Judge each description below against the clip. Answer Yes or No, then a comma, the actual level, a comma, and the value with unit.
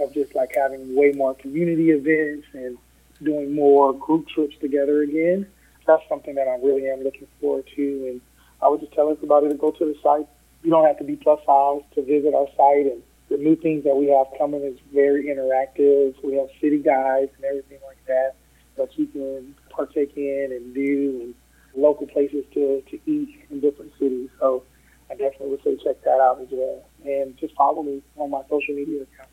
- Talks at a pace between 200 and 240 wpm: Yes, fast, 205 wpm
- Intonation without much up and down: Yes, narrow, 1.7 semitones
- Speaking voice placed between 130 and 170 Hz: Yes, medium, 140 Hz